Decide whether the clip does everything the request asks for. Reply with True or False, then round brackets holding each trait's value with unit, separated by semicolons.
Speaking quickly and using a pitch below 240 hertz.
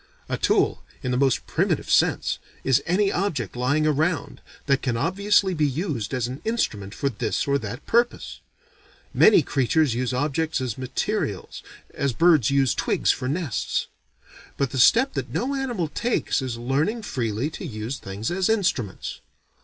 False (160 wpm; 140 Hz)